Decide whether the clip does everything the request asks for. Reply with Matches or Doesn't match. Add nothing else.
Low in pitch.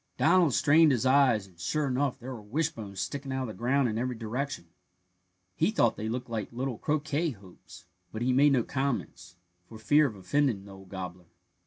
Matches